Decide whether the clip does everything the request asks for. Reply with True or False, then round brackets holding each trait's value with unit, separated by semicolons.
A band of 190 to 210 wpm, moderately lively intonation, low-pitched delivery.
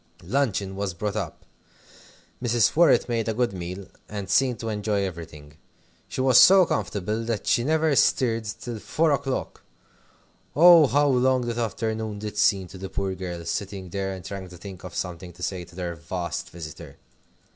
False (175 wpm; 4.7 semitones; 105 Hz)